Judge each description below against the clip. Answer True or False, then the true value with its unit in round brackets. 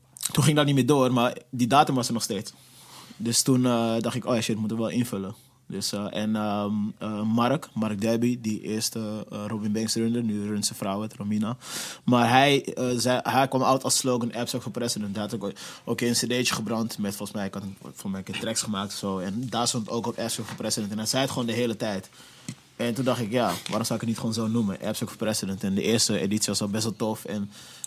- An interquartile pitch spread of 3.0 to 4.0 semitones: False (2.5 semitones)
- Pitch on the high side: False (115 Hz)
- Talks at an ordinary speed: False (250 wpm)